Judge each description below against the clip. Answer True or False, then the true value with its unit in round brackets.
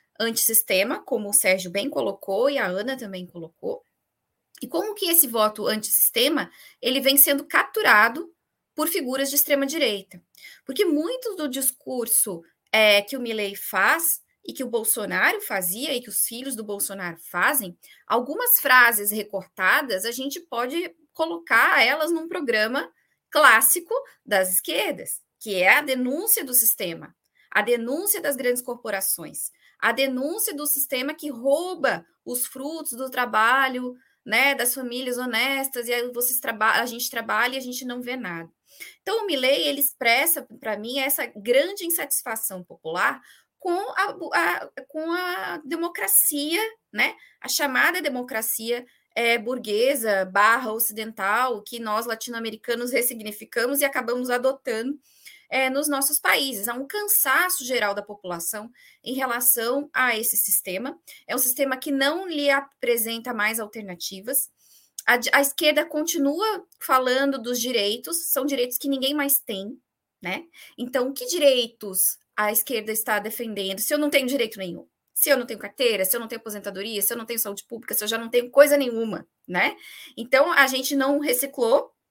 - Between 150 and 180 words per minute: True (155 wpm)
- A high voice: True (255 Hz)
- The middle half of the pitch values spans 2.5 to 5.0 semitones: True (4.2 semitones)